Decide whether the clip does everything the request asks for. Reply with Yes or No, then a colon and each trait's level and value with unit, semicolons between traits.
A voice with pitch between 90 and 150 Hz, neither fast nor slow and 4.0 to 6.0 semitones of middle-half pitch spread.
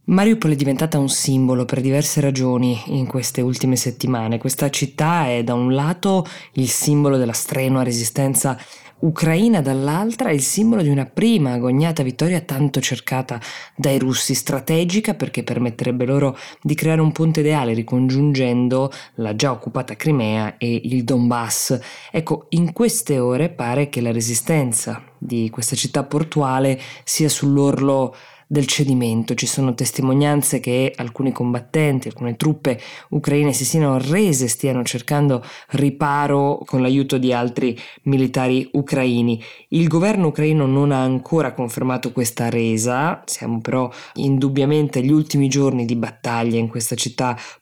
No: low, 135 Hz; average, 140 wpm; average, 3.0 semitones